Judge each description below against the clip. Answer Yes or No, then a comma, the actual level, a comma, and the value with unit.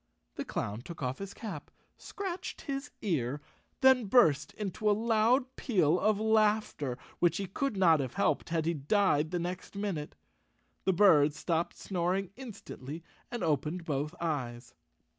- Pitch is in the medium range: Yes, medium, 180 Hz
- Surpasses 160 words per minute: No, average, 155 wpm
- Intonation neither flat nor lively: No, wide, 6.1 semitones